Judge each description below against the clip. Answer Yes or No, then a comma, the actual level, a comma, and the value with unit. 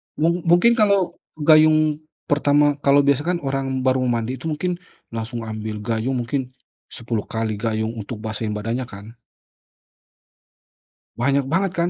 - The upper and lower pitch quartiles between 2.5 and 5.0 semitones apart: No, wide, 5.4 semitones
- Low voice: Yes, low, 130 Hz